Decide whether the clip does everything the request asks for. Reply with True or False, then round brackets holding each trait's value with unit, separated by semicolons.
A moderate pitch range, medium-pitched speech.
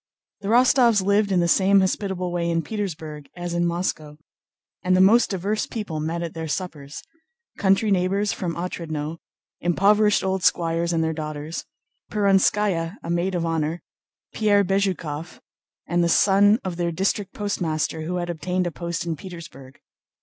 True (3.1 semitones; 175 Hz)